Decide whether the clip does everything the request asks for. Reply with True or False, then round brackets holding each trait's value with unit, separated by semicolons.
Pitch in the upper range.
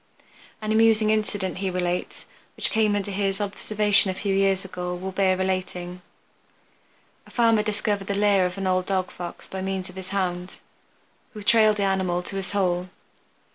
True (195 Hz)